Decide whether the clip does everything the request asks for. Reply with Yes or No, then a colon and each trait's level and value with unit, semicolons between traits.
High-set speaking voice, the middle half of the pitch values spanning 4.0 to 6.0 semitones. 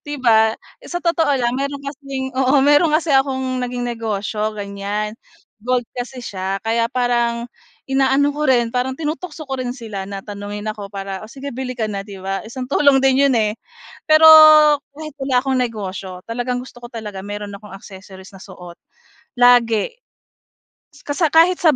Yes: high, 245 Hz; average, 4.5 semitones